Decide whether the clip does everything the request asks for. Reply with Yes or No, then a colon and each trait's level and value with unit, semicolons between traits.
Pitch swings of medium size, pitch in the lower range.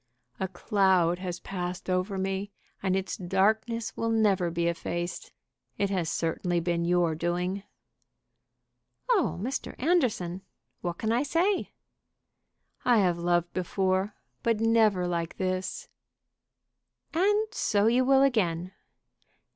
No: average, 4.3 semitones; high, 190 Hz